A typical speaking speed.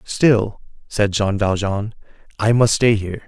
Yes: average, 145 wpm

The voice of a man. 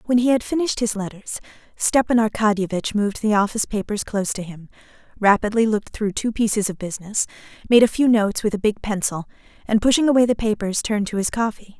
No: female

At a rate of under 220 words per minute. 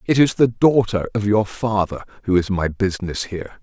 Yes: average, 200 wpm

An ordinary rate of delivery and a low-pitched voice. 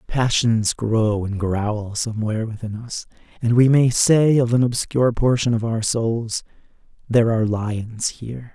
Yes: average, 155 wpm; low, 115 Hz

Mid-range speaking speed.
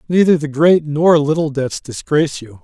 Yes: average, 180 wpm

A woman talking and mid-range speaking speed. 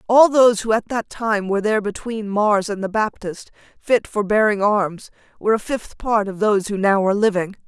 No: female; fast, 210 wpm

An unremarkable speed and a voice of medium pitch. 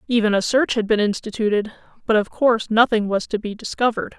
No: average, 185 wpm; high, 220 Hz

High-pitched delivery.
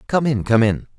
No: low, 120 Hz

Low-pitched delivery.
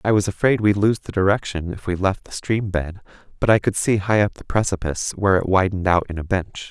Yes: very low, 95 Hz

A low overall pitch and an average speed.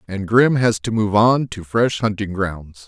No: low, 105 Hz; fast, 210 wpm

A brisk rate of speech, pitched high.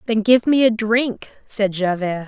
No: average, 185 wpm; high, 215 Hz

